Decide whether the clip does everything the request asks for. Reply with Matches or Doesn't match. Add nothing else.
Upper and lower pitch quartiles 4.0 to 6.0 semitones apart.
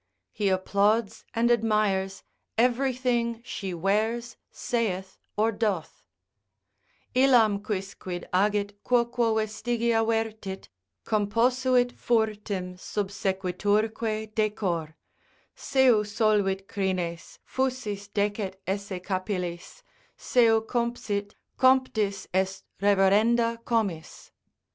Doesn't match